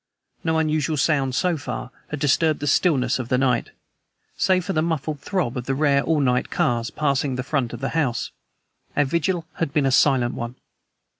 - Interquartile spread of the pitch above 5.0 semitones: No, average, 3.6 semitones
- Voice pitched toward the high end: No, medium, 140 Hz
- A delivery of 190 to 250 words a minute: Yes, average, 195 wpm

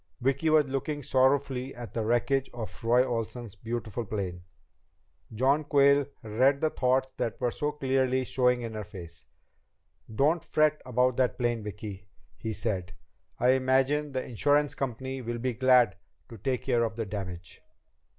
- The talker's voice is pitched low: Yes, low, 125 Hz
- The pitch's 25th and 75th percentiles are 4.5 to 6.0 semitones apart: No, average, 3.2 semitones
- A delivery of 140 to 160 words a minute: Yes, average, 155 wpm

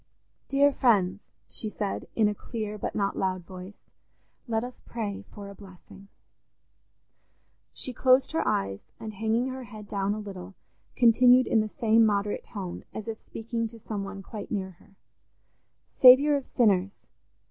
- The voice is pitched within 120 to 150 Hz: No, high, 215 Hz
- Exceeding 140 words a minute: Yes, average, 160 wpm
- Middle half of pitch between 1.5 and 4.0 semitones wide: Yes, average, 2.9 semitones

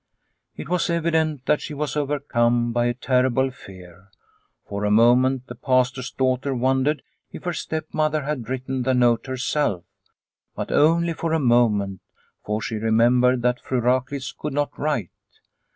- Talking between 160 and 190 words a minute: No, average, 150 wpm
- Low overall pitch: Yes, low, 130 Hz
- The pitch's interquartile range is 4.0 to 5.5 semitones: No, average, 3.5 semitones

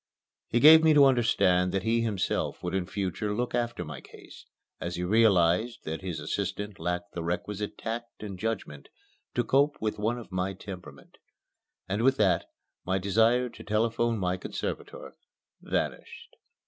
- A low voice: Yes, low, 105 Hz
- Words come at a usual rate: Yes, average, 160 wpm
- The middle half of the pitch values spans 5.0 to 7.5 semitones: No, average, 4.3 semitones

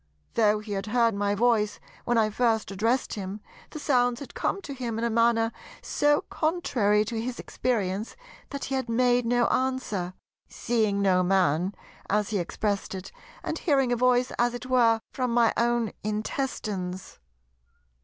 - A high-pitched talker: Yes, high, 230 Hz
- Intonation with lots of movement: No, average, 3.2 semitones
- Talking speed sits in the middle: Yes, average, 165 wpm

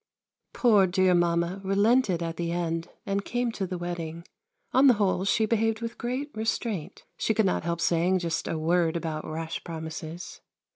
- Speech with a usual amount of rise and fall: Yes, average, 4.4 semitones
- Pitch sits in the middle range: Yes, medium, 180 Hz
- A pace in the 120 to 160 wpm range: No, average, 175 wpm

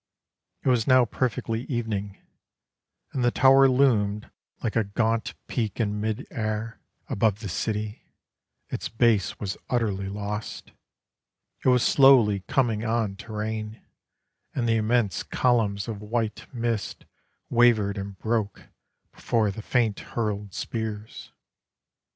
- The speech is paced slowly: Yes, slow, 125 wpm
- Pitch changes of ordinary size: No, narrow, 2.3 semitones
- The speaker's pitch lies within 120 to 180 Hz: No, low, 110 Hz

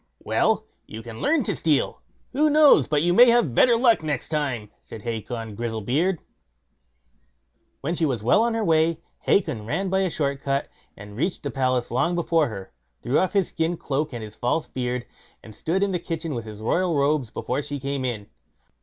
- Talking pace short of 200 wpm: Yes, average, 190 wpm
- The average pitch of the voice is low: No, medium, 145 Hz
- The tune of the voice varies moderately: No, wide, 6.5 semitones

